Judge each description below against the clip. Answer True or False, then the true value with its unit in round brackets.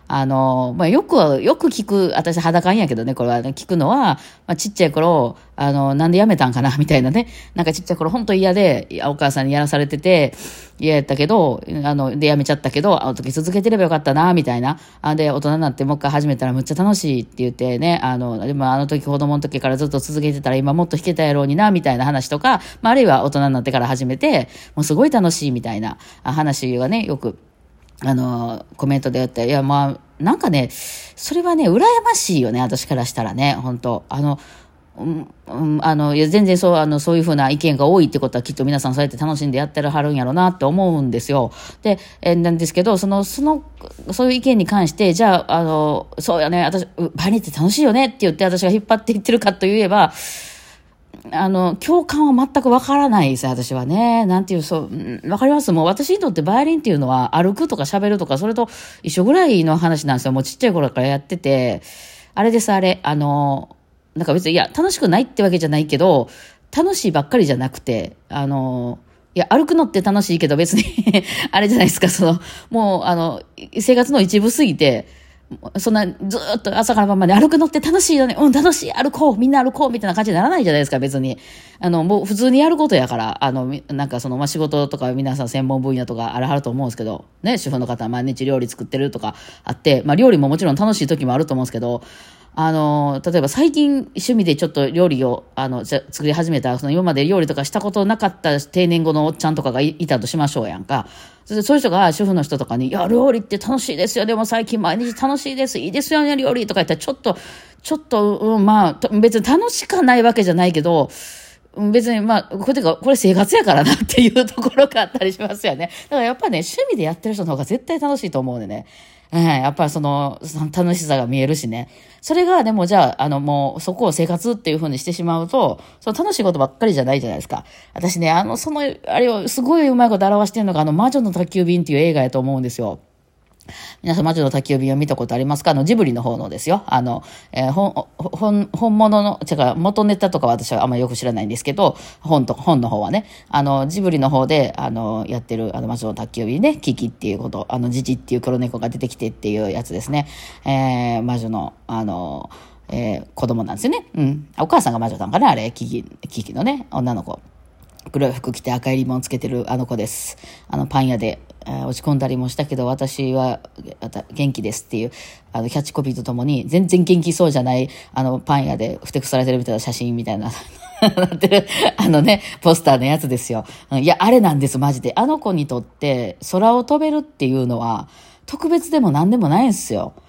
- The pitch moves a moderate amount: False (7.7 semitones)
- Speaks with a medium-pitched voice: True (155 Hz)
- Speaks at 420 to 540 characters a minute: True (445 characters per minute)